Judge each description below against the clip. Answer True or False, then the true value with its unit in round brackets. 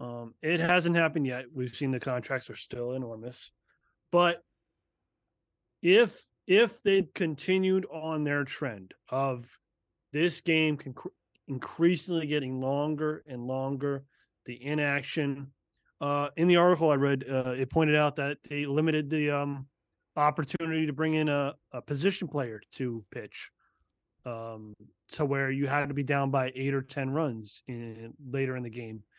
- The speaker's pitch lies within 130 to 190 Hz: True (140 Hz)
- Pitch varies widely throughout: False (3.4 semitones)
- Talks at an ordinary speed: True (150 wpm)